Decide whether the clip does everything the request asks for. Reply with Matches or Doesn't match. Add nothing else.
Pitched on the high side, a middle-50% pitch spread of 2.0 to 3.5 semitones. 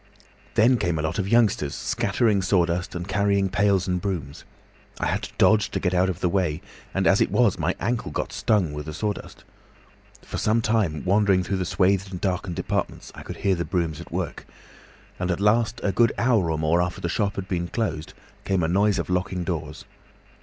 Doesn't match